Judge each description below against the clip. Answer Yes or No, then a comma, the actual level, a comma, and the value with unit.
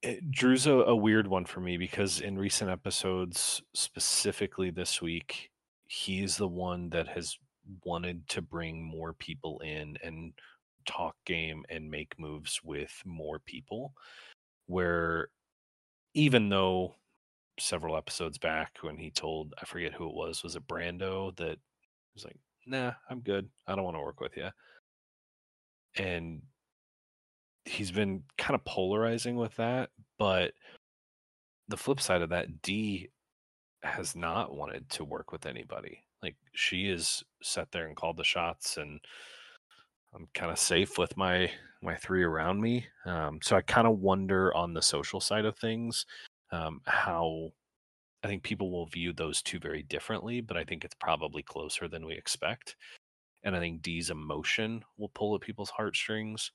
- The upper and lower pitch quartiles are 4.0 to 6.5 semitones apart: Yes, average, 4.7 semitones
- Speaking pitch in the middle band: No, very low, 95 Hz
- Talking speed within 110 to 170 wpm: Yes, average, 160 wpm